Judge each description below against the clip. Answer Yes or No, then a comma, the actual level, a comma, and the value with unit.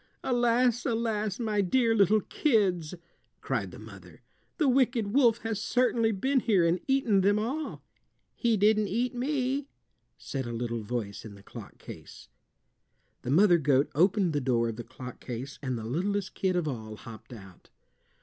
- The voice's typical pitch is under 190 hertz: No, high, 200 Hz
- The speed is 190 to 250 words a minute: No, average, 165 wpm